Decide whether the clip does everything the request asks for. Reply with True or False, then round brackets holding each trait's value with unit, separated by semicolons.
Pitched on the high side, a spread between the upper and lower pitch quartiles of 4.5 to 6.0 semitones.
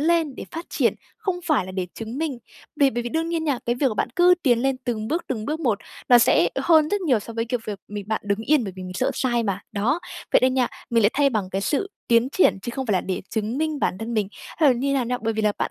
True (245 Hz; 5.5 semitones)